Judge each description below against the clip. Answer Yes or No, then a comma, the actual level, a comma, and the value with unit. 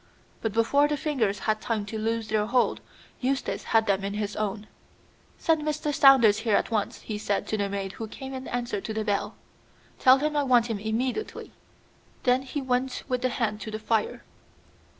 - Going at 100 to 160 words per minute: No, average, 195 wpm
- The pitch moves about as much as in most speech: Yes, average, 3.7 semitones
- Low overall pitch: No, high, 225 Hz